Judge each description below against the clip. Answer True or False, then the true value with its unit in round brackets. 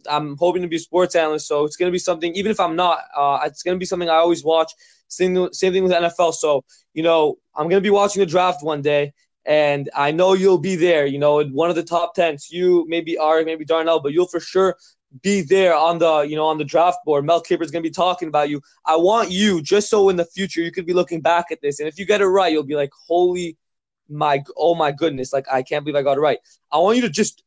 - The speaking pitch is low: False (170 Hz)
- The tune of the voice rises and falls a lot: False (3.2 semitones)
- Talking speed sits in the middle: False (270 wpm)